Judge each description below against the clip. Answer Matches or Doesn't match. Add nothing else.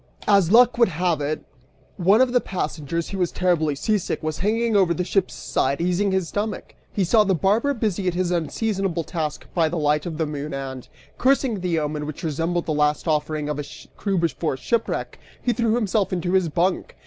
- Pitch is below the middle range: Doesn't match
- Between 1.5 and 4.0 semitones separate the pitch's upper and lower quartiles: Doesn't match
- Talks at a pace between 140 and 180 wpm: Doesn't match